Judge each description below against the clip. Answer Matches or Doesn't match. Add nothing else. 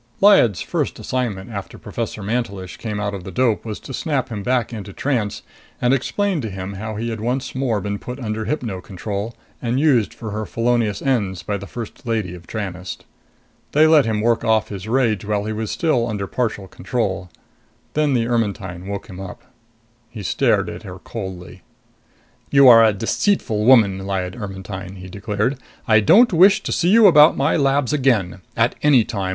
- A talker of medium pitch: Doesn't match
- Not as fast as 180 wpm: Doesn't match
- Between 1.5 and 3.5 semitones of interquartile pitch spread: Doesn't match